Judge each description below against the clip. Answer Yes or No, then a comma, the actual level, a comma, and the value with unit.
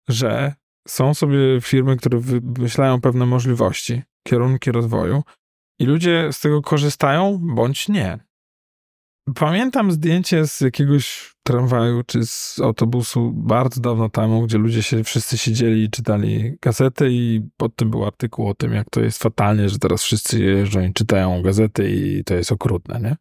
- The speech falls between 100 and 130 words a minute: No, average, 155 wpm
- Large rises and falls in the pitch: No, average, 3.8 semitones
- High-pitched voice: No, low, 120 Hz